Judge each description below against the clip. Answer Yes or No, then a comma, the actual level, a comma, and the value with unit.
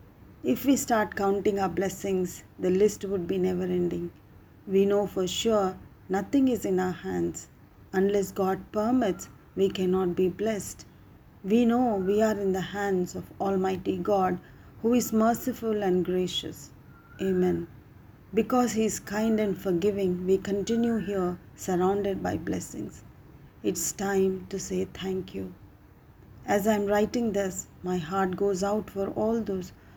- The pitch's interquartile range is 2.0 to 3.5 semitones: Yes, narrow, 2.4 semitones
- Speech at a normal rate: Yes, average, 150 wpm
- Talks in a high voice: Yes, high, 195 Hz